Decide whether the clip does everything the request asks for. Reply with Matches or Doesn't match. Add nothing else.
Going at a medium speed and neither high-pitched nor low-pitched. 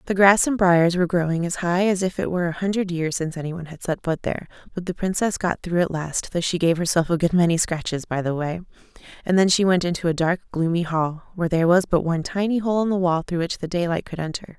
Doesn't match